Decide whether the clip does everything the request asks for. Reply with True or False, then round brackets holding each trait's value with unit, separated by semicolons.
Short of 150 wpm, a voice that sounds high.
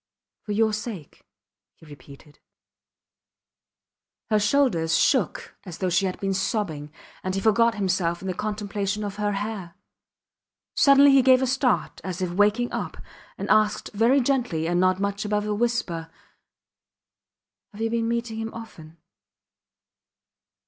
True (140 wpm; 205 Hz)